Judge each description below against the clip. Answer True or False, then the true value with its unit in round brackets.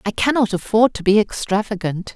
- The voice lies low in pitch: False (210 Hz)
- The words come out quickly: False (165 wpm)